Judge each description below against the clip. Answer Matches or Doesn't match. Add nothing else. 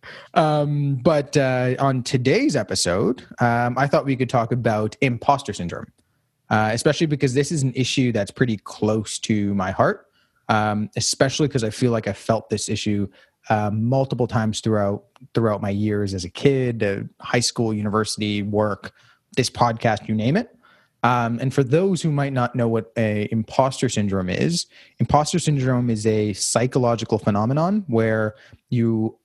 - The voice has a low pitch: Matches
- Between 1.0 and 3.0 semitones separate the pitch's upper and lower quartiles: Doesn't match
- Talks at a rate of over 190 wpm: Doesn't match